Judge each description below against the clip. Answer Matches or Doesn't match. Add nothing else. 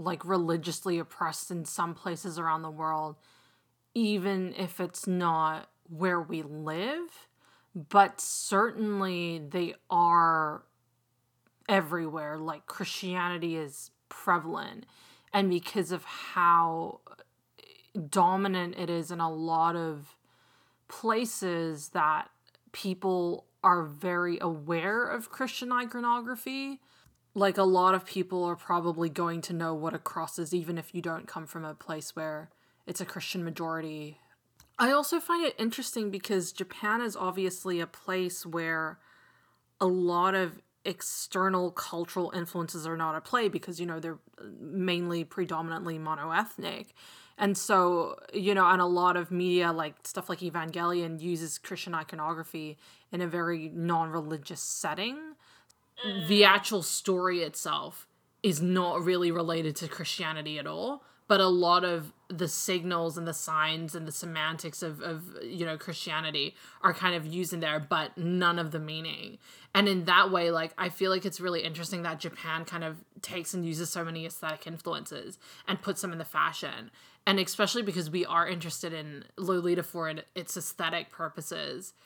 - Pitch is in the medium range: Matches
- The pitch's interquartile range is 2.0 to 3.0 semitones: Matches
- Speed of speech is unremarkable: Matches